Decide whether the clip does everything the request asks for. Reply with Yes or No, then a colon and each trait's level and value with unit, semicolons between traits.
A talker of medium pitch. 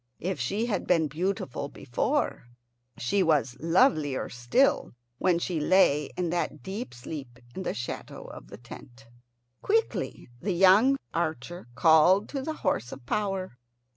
Yes: medium, 170 Hz